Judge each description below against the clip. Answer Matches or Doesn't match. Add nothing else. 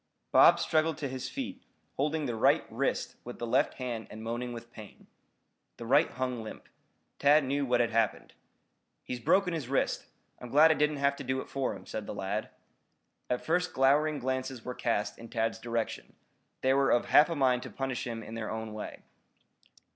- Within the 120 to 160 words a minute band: Doesn't match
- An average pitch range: Matches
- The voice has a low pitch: Matches